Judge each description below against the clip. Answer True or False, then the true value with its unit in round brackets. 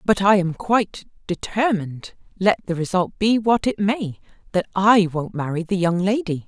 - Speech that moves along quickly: False (175 wpm)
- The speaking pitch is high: True (195 Hz)